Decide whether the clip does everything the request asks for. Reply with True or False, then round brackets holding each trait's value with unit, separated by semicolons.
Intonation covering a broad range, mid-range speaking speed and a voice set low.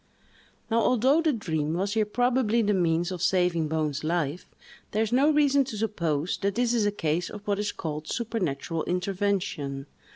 False (5.7 semitones; 175 wpm; 195 Hz)